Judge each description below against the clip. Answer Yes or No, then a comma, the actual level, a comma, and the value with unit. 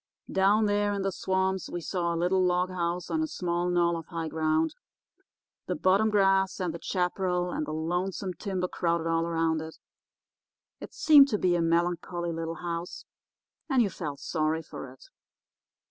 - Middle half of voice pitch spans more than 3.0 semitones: No, narrow, 2.5 semitones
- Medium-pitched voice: Yes, medium, 175 Hz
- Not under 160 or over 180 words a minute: Yes, average, 175 wpm